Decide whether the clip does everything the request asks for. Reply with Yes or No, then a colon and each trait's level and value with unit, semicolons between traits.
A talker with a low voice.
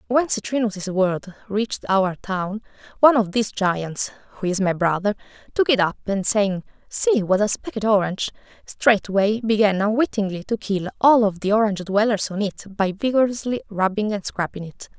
No: high, 205 Hz